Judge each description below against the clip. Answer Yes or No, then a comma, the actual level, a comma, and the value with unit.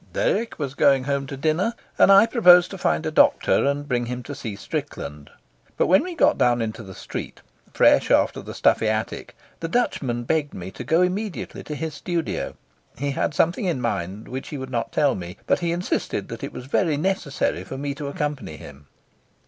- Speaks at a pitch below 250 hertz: Yes, medium, 140 Hz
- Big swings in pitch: Yes, wide, 6.2 semitones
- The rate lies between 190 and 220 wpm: Yes, fast, 205 wpm